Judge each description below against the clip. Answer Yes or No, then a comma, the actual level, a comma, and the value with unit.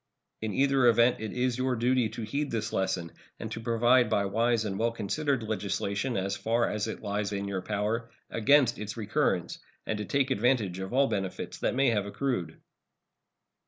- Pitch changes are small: No, average, 3.5 semitones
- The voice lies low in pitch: Yes, low, 110 Hz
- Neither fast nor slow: Yes, average, 185 wpm